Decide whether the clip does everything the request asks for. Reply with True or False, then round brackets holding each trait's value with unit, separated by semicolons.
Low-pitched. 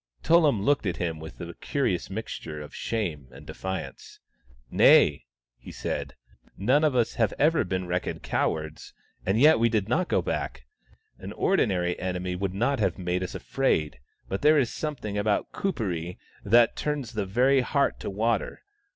True (100 Hz)